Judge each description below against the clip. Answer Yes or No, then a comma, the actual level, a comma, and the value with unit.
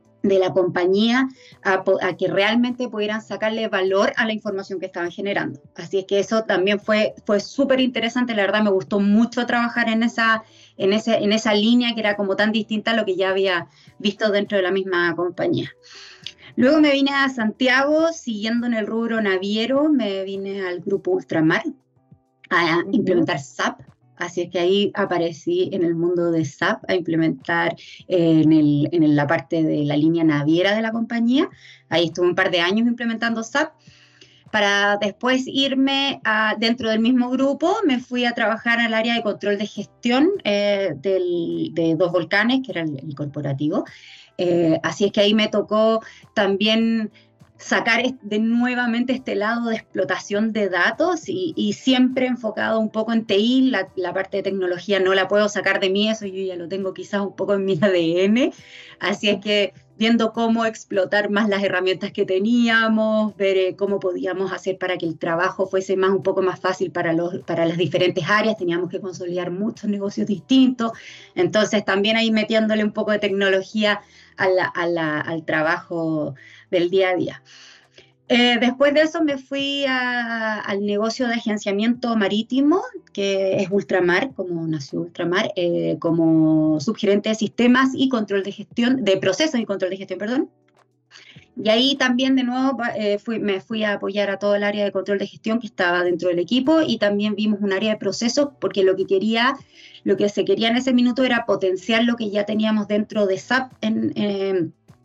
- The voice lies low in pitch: No, high, 205 Hz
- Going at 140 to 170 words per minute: No, average, 185 wpm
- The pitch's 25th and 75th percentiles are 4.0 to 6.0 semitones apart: No, average, 3.6 semitones